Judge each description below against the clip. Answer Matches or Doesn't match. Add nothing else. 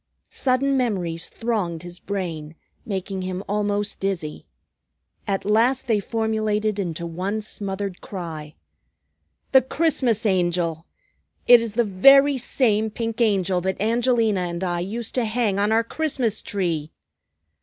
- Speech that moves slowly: Matches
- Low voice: Doesn't match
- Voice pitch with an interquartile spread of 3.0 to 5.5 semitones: Matches